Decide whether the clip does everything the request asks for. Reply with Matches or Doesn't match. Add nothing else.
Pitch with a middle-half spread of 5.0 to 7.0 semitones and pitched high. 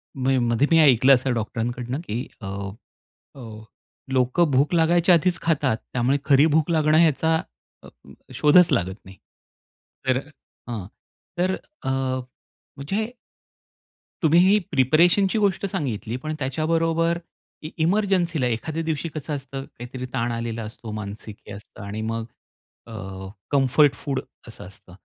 Doesn't match